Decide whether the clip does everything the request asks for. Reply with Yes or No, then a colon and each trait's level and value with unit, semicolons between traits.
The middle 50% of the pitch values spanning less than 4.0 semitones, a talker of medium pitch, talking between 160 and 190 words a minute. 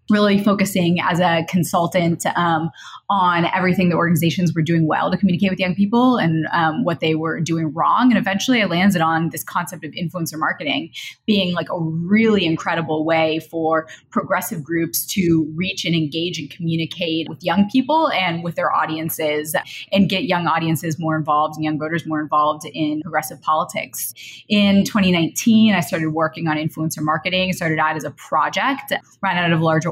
Yes: average, 2.8 semitones; medium, 170 Hz; average, 180 wpm